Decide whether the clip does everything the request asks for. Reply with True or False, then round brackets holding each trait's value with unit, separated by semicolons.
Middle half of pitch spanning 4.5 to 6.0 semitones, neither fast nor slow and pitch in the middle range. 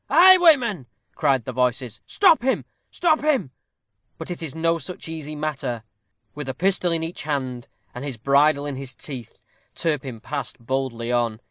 True (5.0 semitones; 165 wpm; 145 Hz)